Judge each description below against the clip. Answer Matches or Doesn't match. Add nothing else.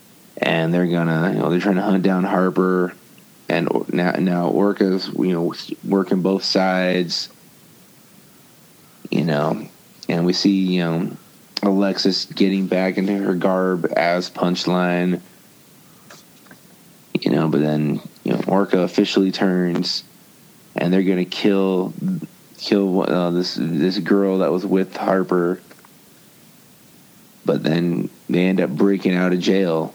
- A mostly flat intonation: Matches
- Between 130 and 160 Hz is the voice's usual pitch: Doesn't match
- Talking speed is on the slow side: Matches